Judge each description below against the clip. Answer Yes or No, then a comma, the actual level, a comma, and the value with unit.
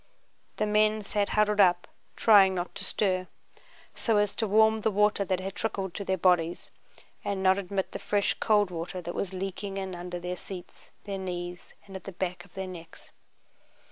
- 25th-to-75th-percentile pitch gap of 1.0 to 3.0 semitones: Yes, narrow, 2.4 semitones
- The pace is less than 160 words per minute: No, average, 190 wpm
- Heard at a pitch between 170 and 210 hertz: Yes, high, 190 Hz